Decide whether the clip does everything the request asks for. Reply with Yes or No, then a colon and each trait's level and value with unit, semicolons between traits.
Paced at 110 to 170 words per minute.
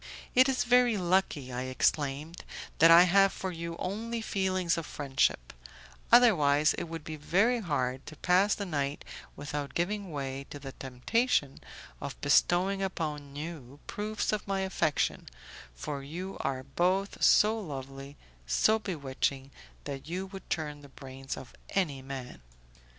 Yes: average, 145 wpm